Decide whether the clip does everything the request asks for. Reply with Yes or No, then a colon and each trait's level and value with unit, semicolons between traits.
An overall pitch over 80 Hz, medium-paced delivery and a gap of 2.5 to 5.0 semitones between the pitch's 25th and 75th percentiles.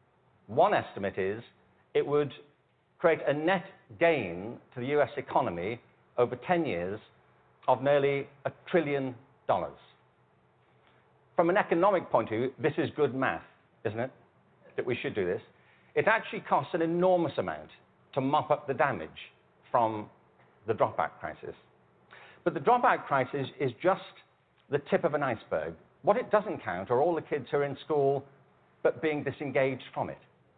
Yes: medium, 140 Hz; average, 160 wpm; average, 4.4 semitones